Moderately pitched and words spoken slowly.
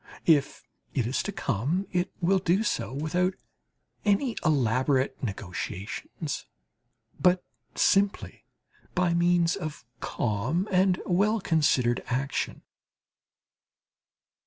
Yes: medium, 170 Hz; slow, 95 wpm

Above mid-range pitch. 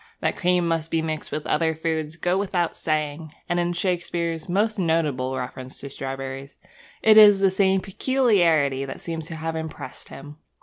No: medium, 165 Hz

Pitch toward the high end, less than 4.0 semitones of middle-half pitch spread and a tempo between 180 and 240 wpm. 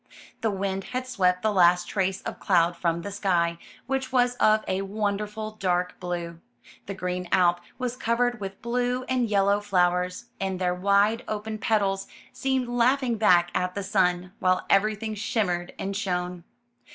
No: high, 195 Hz; average, 3.4 semitones; average, 165 wpm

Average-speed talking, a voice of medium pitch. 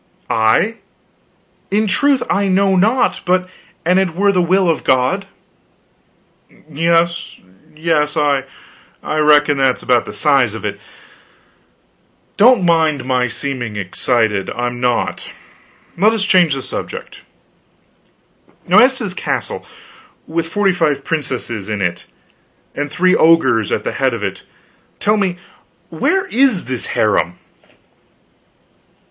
No: slow, 125 wpm; medium, 160 Hz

